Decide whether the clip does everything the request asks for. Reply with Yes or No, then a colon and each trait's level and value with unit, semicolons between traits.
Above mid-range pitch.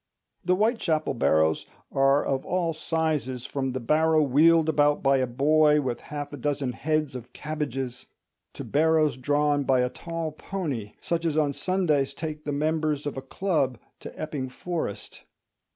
No: medium, 150 Hz